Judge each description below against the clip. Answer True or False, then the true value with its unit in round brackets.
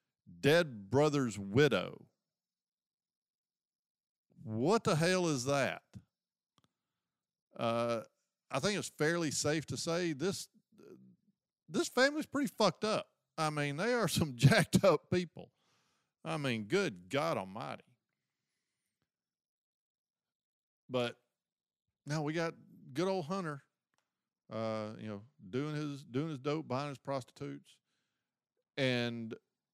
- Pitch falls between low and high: True (150 Hz)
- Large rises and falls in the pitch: True (6.4 semitones)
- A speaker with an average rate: False (110 wpm)